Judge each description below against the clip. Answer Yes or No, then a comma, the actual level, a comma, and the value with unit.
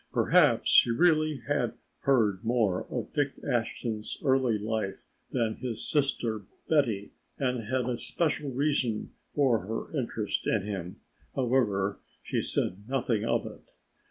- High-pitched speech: No, low, 120 Hz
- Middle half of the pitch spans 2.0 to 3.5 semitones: No, average, 4.1 semitones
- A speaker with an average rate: No, slow, 130 wpm